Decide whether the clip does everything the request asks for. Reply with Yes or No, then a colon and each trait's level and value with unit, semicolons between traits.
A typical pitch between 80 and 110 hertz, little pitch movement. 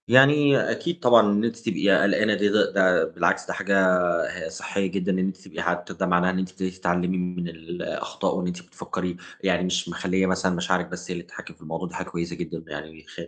Yes: very low, 95 Hz; narrow, 2.1 semitones